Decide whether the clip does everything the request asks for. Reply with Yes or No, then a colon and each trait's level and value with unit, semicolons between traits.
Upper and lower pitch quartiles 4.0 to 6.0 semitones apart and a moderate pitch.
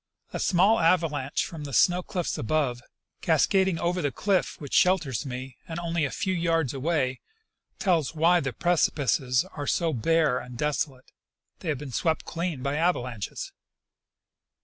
Yes: average, 4.6 semitones; medium, 155 Hz